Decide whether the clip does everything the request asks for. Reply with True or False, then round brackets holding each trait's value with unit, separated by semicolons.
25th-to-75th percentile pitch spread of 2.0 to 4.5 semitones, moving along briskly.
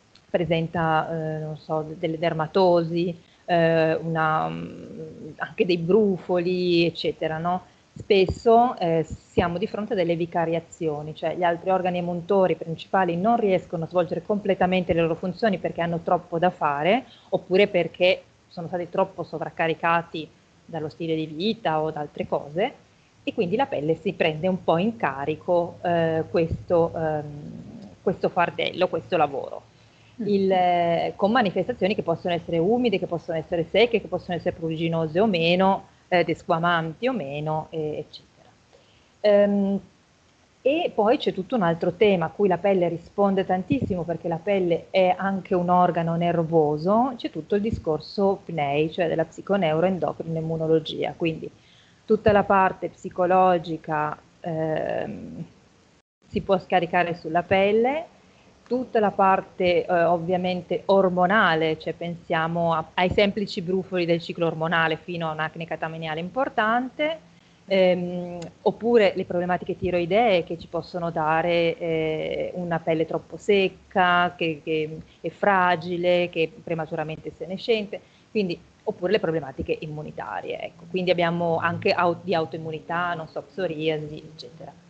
False (2.7 semitones; 140 wpm)